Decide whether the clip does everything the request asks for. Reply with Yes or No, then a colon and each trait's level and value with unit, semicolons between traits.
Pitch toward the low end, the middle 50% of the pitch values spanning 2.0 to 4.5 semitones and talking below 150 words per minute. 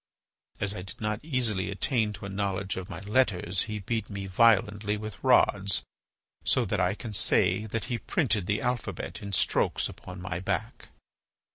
No: low, 100 Hz; narrow, 2.4 semitones; average, 170 wpm